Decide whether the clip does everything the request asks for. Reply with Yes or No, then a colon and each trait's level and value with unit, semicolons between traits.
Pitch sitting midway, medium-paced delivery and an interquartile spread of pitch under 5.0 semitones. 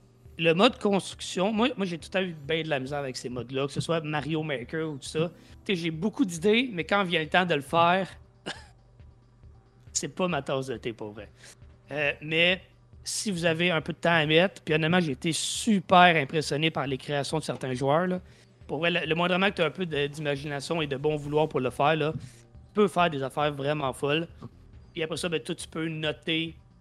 No: medium, 155 Hz; fast, 230 wpm; average, 3.7 semitones